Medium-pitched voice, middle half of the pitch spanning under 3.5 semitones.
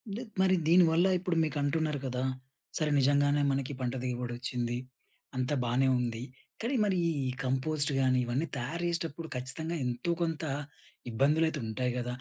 No: medium, 145 Hz; average, 4.6 semitones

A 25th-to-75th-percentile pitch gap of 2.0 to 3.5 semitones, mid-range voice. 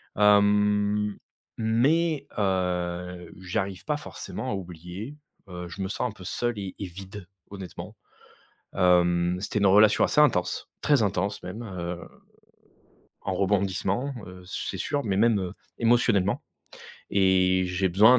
No: average, 2.8 semitones; low, 100 Hz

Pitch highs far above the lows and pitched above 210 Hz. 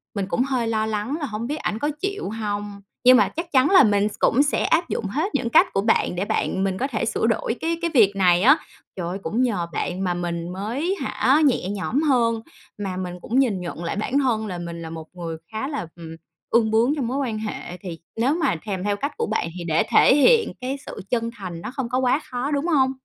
Yes: wide, 6.1 semitones; high, 225 Hz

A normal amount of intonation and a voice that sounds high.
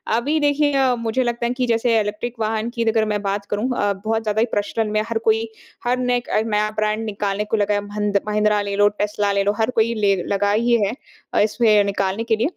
No: narrow, 2.1 semitones; high, 215 Hz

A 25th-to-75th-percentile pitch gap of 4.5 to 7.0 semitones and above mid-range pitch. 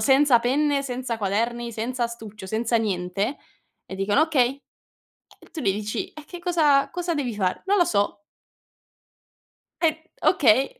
Yes: wide, 5.4 semitones; high, 245 Hz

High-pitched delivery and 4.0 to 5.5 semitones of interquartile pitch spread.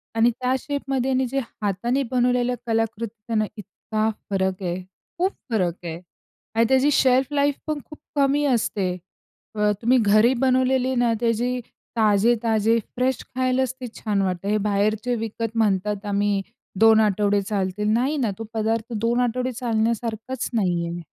No: high, 225 Hz; average, 3.4 semitones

